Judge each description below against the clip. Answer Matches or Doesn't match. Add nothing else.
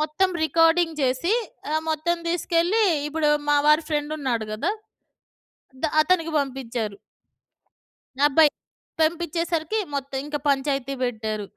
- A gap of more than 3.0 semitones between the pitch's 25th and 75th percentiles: Matches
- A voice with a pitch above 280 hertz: Matches